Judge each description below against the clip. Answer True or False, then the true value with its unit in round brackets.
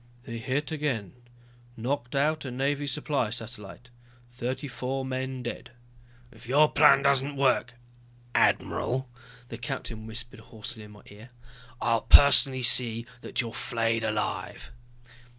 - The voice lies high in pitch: False (125 Hz)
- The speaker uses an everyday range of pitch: True (3.1 semitones)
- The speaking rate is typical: False (130 wpm)